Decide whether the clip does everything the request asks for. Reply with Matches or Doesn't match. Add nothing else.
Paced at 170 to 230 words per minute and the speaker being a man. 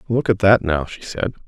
Doesn't match